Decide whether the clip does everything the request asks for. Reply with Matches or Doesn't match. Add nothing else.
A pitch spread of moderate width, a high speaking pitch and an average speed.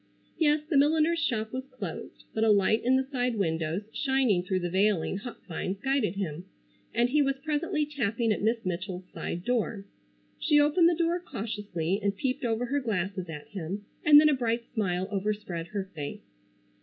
Doesn't match